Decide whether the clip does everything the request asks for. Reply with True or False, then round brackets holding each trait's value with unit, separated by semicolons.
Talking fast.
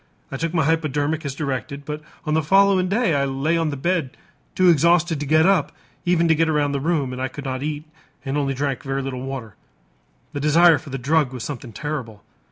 True (225 wpm)